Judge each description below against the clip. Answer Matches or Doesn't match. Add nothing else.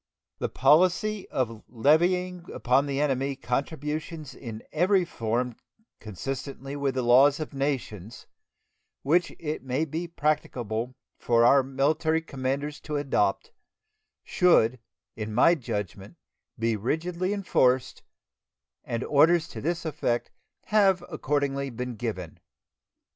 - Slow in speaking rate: Matches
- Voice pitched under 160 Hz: Matches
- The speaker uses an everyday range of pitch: Matches